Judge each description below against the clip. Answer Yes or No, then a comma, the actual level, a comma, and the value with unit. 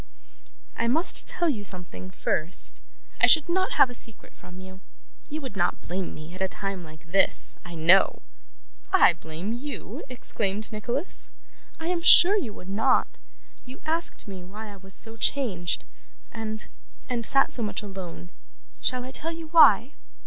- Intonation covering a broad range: Yes, wide, 6.7 semitones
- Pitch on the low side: No, high, 215 Hz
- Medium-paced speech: Yes, average, 165 wpm